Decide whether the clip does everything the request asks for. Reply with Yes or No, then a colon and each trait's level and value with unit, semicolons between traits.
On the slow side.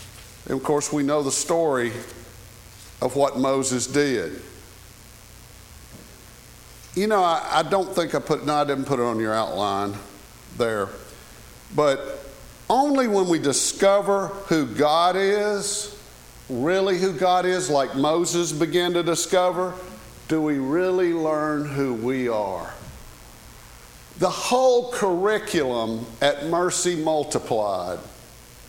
Yes: slow, 120 wpm